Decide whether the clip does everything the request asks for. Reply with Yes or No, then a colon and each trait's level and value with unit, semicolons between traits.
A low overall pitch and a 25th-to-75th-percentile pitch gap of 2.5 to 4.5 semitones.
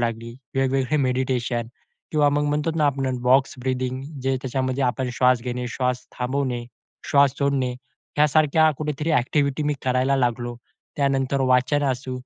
No: low, 130 Hz; narrow, 2.0 semitones